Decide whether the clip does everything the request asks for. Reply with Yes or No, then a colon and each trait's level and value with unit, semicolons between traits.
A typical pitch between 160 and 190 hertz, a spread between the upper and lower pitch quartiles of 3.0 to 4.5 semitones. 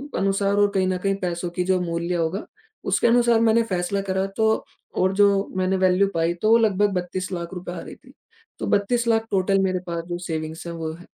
No: medium, 185 Hz; narrow, 2.4 semitones